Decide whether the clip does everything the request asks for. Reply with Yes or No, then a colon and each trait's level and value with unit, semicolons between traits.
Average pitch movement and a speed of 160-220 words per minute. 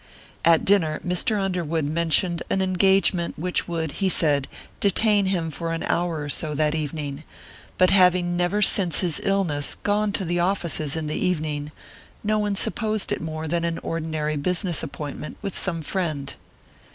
Yes: average, 3.5 semitones; average, 165 wpm